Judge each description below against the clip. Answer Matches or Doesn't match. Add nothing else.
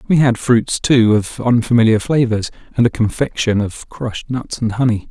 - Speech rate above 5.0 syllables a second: Doesn't match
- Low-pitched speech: Matches